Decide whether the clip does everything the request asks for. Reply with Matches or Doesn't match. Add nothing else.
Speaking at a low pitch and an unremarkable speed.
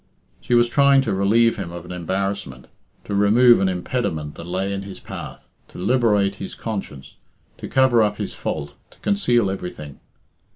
Matches